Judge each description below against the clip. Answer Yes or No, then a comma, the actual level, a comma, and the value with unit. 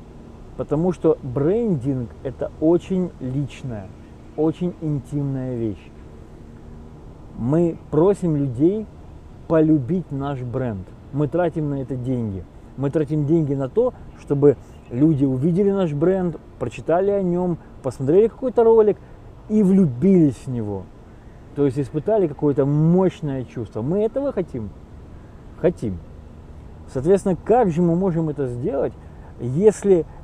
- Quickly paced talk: No, average, 115 wpm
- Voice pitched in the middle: Yes, medium, 145 Hz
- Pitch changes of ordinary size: No, wide, 7.1 semitones